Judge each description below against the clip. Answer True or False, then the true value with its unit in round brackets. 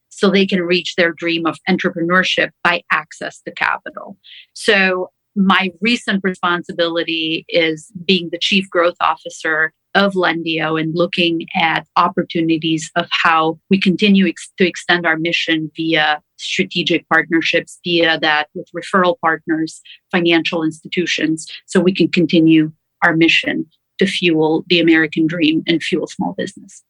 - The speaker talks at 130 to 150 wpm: True (140 wpm)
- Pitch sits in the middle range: True (170 Hz)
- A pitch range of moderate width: False (2.2 semitones)